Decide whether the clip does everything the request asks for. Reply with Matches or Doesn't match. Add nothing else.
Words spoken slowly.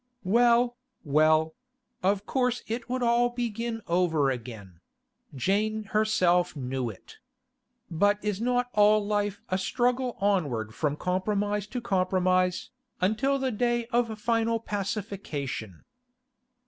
Matches